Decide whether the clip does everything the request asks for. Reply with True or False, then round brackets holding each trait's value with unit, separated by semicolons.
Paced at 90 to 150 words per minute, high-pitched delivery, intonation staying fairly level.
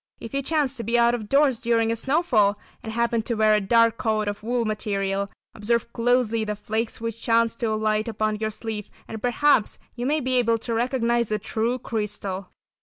False (200 wpm; 230 Hz; 1.9 semitones)